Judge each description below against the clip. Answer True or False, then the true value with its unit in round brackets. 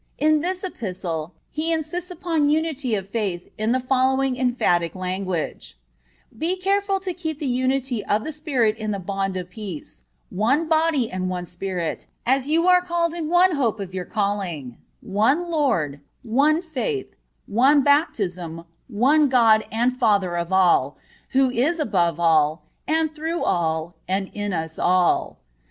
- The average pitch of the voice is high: True (240 Hz)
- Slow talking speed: False (155 wpm)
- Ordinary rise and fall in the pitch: False (9.0 semitones)